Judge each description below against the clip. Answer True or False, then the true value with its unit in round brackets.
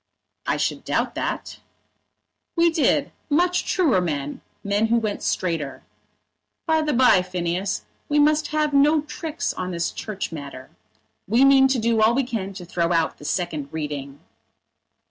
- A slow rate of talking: False (155 wpm)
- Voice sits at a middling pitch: False (215 Hz)